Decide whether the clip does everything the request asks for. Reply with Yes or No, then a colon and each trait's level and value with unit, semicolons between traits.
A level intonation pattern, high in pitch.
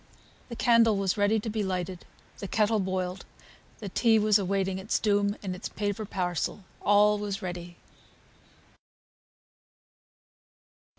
Yes: narrow, 2.1 semitones; high, 200 Hz